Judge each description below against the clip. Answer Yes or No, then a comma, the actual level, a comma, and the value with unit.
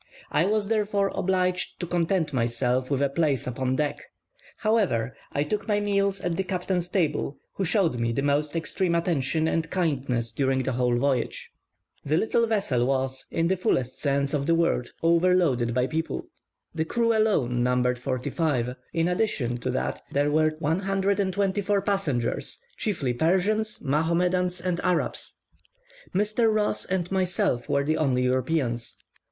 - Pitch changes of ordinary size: No, wide, 6.3 semitones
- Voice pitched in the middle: Yes, medium, 160 Hz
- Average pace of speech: Yes, average, 155 wpm